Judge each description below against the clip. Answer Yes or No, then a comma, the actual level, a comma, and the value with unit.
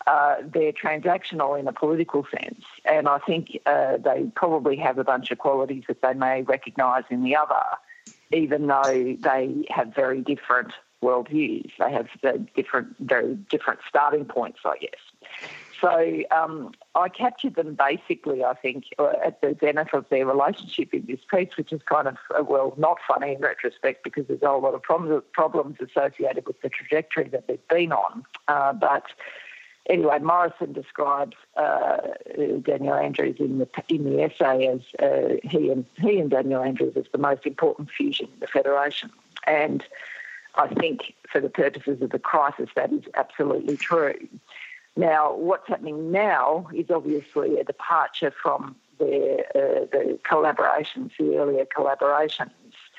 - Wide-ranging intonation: Yes, wide, 8.6 semitones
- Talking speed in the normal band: Yes, average, 160 wpm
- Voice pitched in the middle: Yes, medium, 155 Hz